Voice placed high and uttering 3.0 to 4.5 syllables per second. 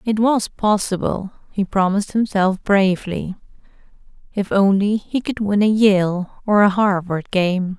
Yes: high, 200 Hz; 4.2 syllables/s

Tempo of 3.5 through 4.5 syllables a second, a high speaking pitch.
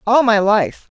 Yes: 3.9 syllables/s; high, 220 Hz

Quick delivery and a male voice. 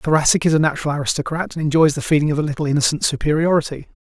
Yes: fast, 225 wpm; male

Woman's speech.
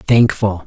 Yes: female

